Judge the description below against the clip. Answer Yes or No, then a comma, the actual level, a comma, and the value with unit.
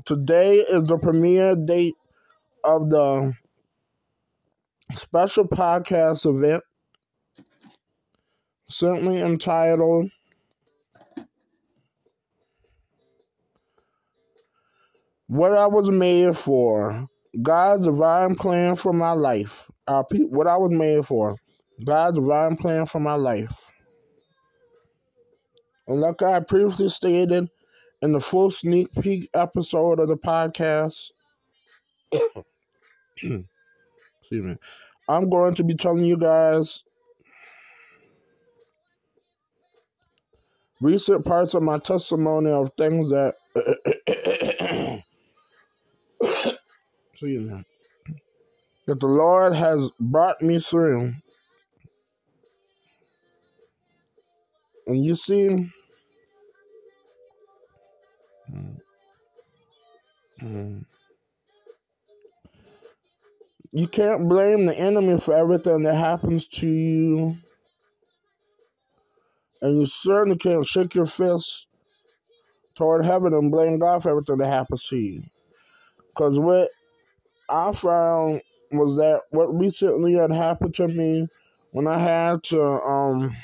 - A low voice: No, medium, 175 Hz